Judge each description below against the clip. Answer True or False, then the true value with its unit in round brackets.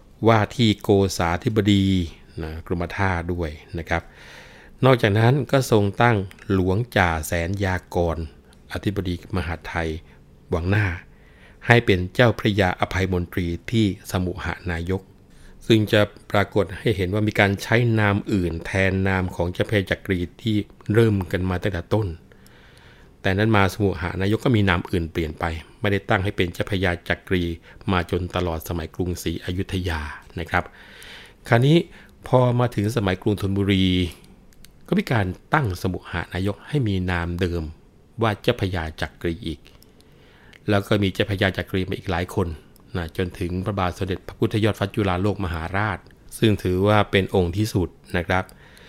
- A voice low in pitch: True (95 Hz)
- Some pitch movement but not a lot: True (3.1 semitones)